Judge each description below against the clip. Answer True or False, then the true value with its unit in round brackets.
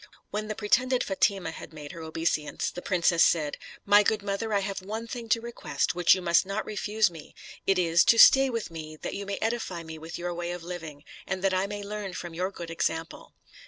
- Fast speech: True (225 wpm)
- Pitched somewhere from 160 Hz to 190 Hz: True (185 Hz)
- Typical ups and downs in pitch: True (3.9 semitones)